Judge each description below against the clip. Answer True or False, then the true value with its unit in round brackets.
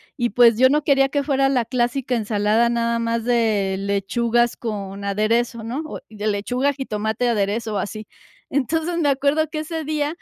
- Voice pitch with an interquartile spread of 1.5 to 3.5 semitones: False (4.1 semitones)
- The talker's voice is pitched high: True (235 Hz)